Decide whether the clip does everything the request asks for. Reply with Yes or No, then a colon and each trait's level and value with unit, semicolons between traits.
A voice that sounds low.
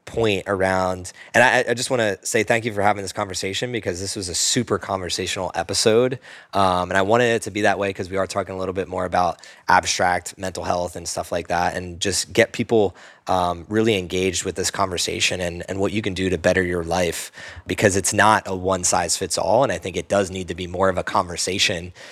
Yes: very low, 95 Hz